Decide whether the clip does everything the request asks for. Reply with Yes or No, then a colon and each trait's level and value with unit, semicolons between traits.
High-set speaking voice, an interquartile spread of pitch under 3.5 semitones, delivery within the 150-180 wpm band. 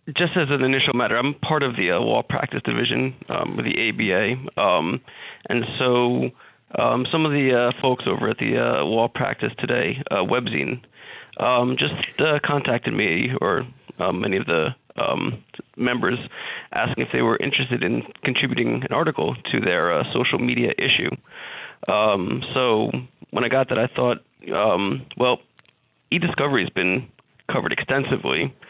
No: low, 130 Hz; average, 2.8 semitones; average, 160 wpm